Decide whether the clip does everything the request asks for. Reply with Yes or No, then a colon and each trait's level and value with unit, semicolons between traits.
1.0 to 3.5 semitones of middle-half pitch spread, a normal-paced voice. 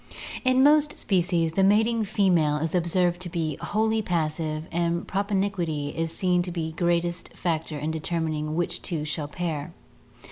Yes: average, 3.1 semitones; average, 165 wpm